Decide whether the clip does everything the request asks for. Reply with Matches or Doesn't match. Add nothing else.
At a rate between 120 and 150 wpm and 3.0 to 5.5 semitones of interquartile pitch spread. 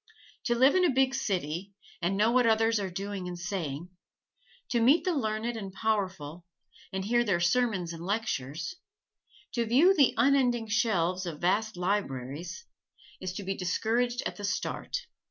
Doesn't match